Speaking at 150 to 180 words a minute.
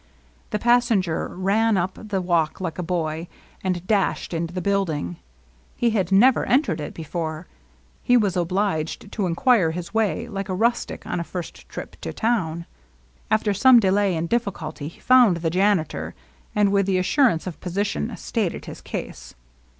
Yes: average, 165 wpm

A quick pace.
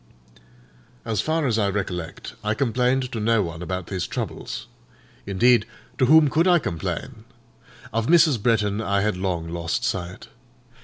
No: average, 150 wpm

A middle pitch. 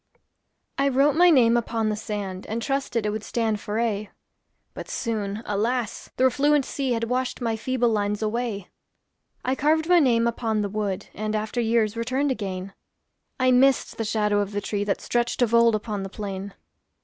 No: high, 225 Hz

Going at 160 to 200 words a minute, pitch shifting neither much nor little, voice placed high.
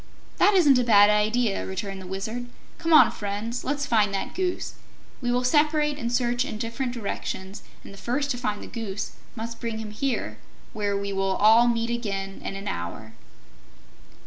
Yes: average, 180 wpm; average, 3.7 semitones; high, 230 Hz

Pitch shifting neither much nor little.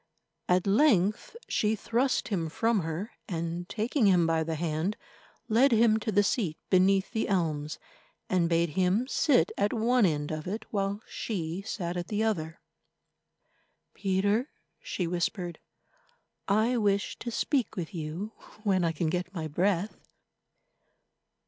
Yes: average, 4.4 semitones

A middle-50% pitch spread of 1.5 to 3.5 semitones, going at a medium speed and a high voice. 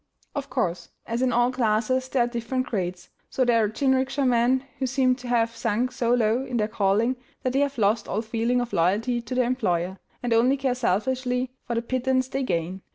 No: average, 2.7 semitones; fast, 210 wpm; high, 245 Hz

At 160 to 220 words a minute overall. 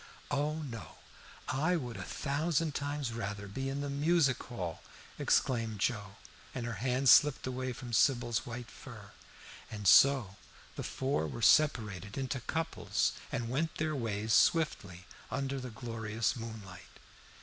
No: average, 140 wpm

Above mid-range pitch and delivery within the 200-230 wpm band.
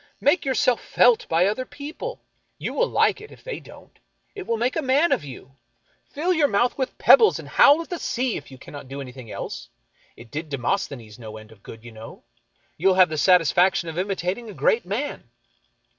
Yes: high, 195 Hz; fast, 205 wpm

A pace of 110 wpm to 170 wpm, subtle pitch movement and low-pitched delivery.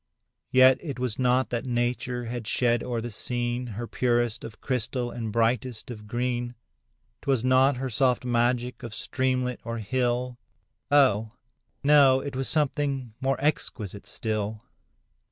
Yes: slow, 135 wpm; narrow, 1.7 semitones; low, 125 Hz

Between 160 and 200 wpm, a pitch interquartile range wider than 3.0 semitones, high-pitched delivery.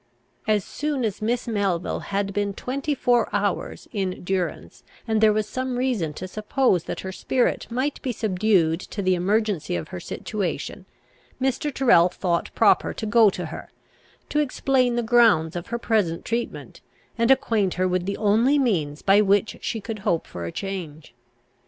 Yes: average, 170 wpm; average, 4.7 semitones; high, 210 Hz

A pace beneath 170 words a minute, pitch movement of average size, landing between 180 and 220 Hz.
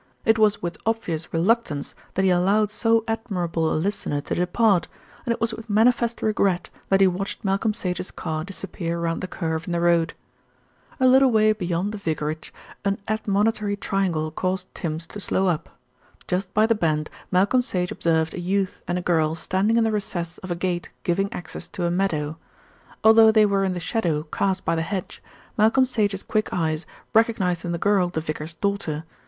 No: average, 190 wpm; average, 4.0 semitones; medium, 185 Hz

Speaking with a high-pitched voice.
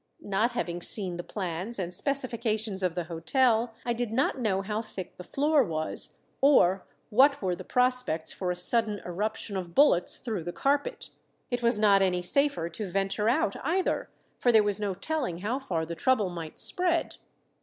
Yes: high, 210 Hz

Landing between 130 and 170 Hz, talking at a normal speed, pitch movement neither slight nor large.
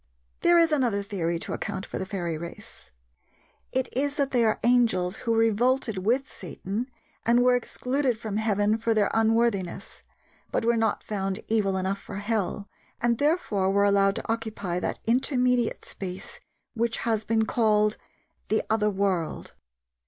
No: high, 220 Hz; average, 155 wpm; average, 3.3 semitones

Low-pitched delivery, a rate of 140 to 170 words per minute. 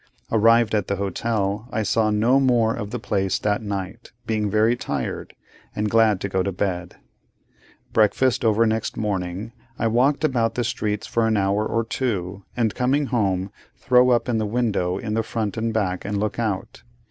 No: low, 110 Hz; average, 180 wpm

